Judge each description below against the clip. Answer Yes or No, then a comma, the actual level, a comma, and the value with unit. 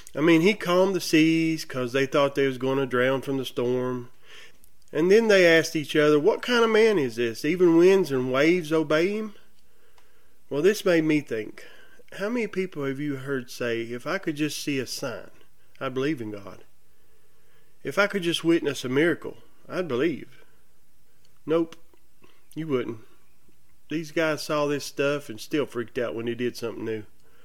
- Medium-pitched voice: Yes, medium, 150 Hz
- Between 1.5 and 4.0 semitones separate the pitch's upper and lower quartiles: No, average, 4.5 semitones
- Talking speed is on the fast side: No, average, 185 wpm